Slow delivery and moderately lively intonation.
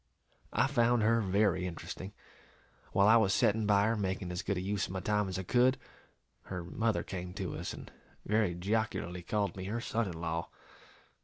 No: average, 190 wpm; average, 3.4 semitones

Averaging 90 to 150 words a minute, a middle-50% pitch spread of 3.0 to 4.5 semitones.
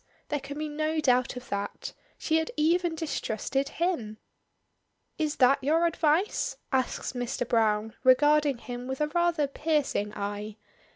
Yes: average, 140 wpm; average, 4.2 semitones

